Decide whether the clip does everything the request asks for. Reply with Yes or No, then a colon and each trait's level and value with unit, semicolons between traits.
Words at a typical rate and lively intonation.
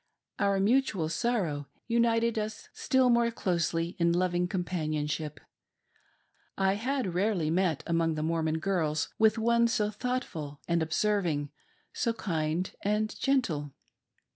No: slow, 125 wpm; wide, 5.7 semitones